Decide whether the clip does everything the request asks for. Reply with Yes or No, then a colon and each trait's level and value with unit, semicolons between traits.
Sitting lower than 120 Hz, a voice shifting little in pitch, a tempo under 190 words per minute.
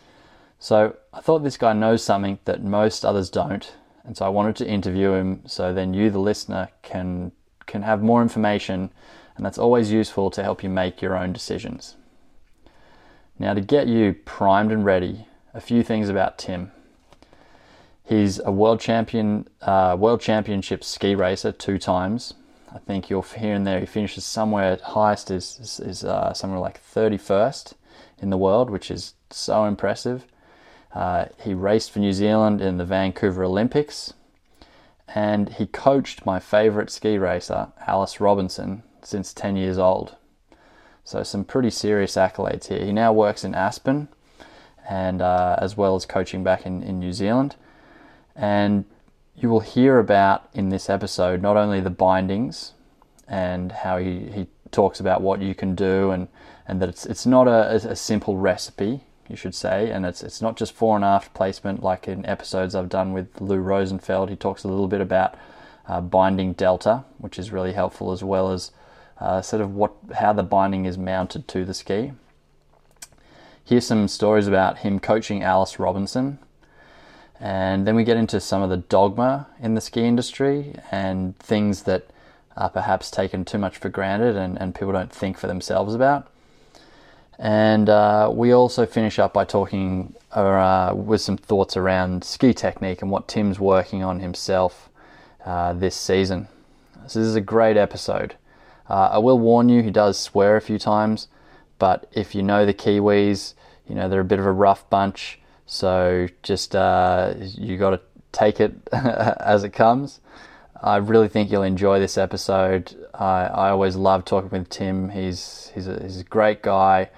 Yes: low, 100 Hz; narrow, 2.3 semitones; average, 175 wpm